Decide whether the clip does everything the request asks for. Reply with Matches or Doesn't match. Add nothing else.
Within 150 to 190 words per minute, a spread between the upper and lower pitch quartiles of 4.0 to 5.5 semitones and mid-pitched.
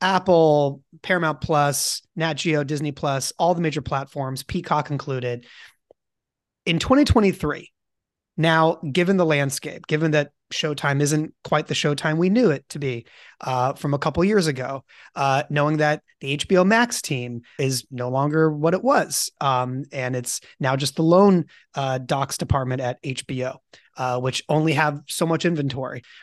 Doesn't match